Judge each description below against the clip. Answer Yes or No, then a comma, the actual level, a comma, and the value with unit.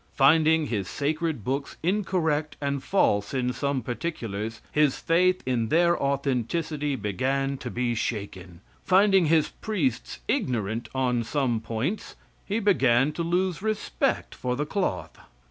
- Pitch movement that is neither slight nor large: No, wide, 5.7 semitones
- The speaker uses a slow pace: Yes, slow, 130 wpm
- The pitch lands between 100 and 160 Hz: Yes, medium, 140 Hz